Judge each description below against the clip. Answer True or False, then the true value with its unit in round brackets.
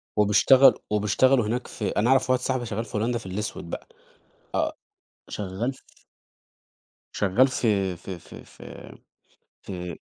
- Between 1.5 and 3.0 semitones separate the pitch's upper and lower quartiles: False (4.4 semitones)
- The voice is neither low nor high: False (110 Hz)